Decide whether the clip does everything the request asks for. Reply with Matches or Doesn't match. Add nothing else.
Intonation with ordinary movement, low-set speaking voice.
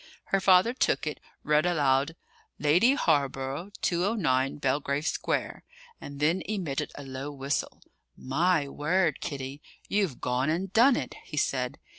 Doesn't match